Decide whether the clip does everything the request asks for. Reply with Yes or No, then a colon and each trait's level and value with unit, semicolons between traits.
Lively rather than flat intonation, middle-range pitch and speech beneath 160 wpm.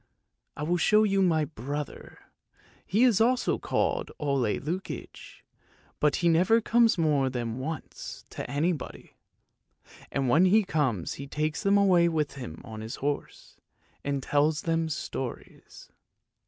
No: average, 4.9 semitones; medium, 155 Hz; average, 140 wpm